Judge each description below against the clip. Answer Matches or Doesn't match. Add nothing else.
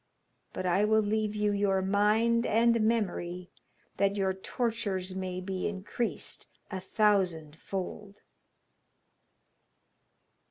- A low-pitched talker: Doesn't match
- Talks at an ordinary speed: Doesn't match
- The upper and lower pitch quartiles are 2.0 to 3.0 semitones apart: Matches